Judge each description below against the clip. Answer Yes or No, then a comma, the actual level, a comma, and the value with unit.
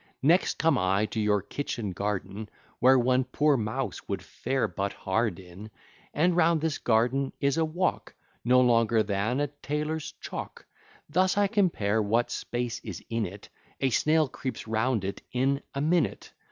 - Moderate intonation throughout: No, wide, 5.8 semitones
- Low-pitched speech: Yes, low, 125 Hz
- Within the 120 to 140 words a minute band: No, average, 165 wpm